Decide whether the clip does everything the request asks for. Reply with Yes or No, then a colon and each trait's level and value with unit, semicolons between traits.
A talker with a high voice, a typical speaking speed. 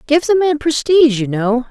No: very high, 280 Hz; fast, 210 wpm